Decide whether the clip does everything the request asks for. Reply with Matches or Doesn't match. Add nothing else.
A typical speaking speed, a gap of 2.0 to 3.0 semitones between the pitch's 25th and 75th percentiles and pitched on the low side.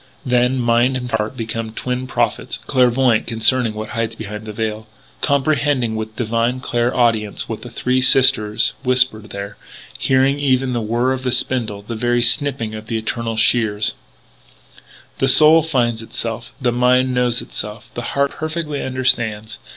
Matches